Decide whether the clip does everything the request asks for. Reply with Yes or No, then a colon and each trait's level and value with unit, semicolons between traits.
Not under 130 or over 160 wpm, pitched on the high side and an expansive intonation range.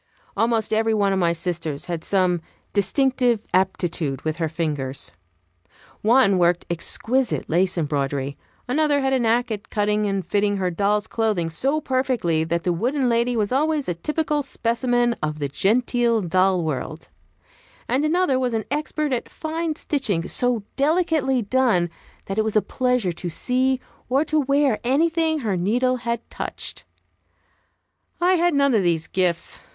Yes: average, 155 wpm; high, 225 Hz; wide, 6.8 semitones